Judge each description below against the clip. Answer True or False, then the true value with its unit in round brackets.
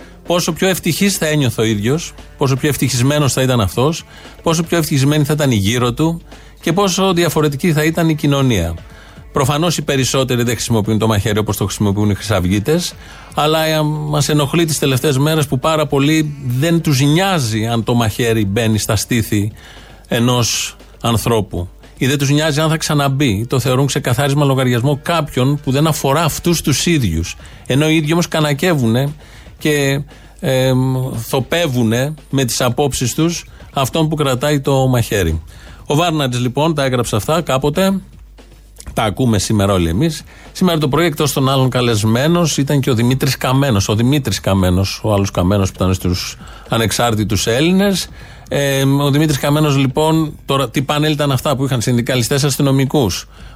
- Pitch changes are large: False (5.0 semitones)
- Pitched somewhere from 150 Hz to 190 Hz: False (135 Hz)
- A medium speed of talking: True (160 wpm)